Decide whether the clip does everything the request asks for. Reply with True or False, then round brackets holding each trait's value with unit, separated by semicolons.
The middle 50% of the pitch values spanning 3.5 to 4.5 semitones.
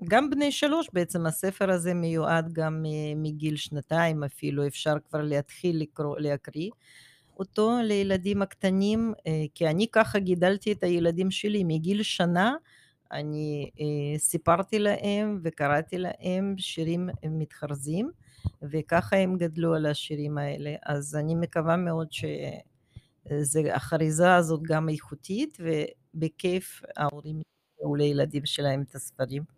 True (4.0 semitones)